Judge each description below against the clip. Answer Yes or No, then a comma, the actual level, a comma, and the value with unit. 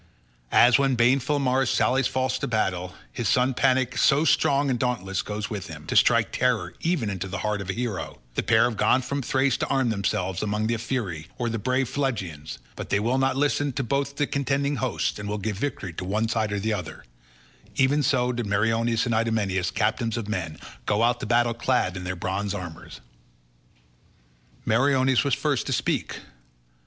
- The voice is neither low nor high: No, low, 115 Hz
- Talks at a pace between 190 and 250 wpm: Yes, average, 195 wpm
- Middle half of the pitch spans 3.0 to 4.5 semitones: No, average, 4.9 semitones